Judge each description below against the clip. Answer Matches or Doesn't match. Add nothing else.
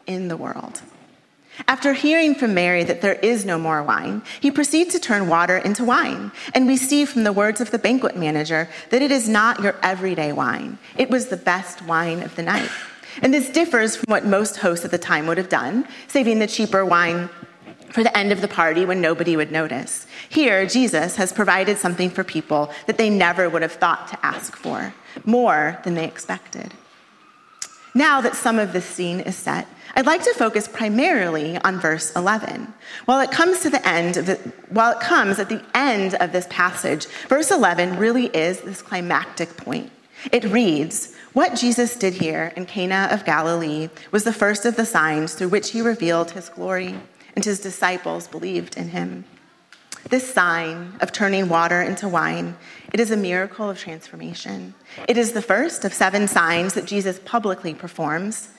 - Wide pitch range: Matches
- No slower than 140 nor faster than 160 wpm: Doesn't match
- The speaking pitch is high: Matches